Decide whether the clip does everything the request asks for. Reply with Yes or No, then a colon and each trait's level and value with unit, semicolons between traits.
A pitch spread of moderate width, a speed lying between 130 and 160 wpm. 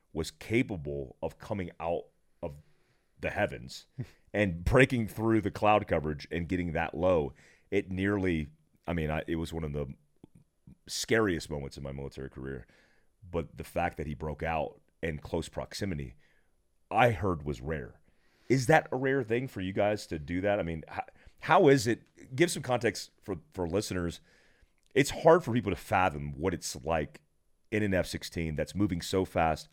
No: average, 5.0 semitones; average, 175 wpm